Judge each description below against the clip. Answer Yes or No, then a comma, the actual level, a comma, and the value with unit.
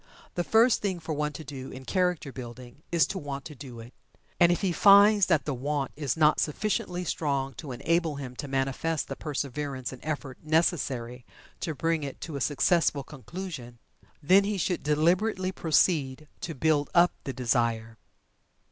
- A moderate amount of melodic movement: Yes, average, 4.4 semitones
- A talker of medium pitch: Yes, medium, 150 Hz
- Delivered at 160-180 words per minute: Yes, average, 175 wpm